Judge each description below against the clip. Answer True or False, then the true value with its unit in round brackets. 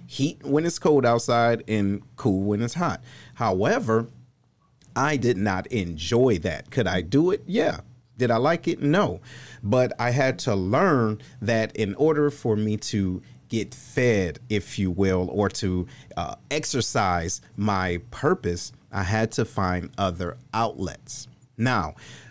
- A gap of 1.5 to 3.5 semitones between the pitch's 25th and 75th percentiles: False (4.5 semitones)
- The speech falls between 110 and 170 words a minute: True (150 wpm)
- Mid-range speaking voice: False (115 Hz)